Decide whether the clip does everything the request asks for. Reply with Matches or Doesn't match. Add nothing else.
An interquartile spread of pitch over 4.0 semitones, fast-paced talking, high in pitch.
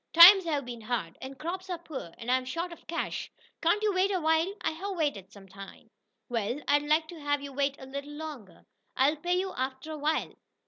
Matches